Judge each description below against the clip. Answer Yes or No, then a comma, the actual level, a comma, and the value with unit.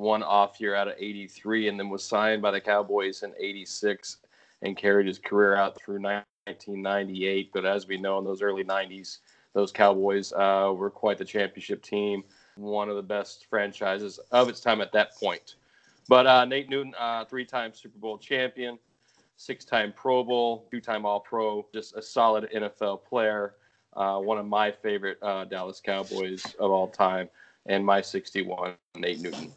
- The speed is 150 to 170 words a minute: No, average, 180 wpm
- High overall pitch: No, low, 100 Hz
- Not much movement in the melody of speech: Yes, narrow, 1.8 semitones